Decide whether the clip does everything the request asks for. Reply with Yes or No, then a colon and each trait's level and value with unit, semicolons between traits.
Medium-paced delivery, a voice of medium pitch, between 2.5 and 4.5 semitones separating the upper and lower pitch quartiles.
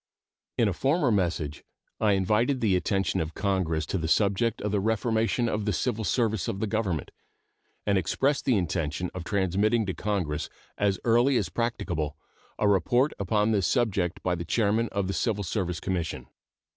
No: average, 170 wpm; low, 100 Hz; average, 3.8 semitones